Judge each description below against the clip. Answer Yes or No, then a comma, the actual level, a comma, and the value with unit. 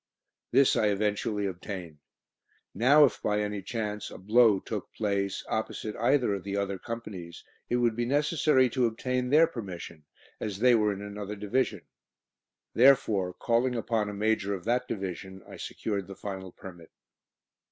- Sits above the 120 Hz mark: No, low, 105 Hz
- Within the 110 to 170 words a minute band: Yes, average, 155 wpm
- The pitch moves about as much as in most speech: Yes, average, 3.6 semitones